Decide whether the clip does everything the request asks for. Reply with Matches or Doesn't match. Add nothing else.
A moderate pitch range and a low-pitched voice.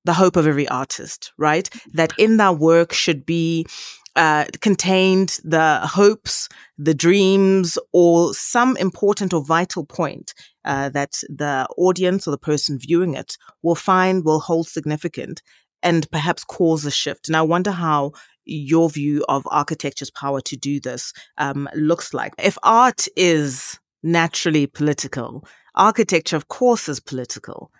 Doesn't match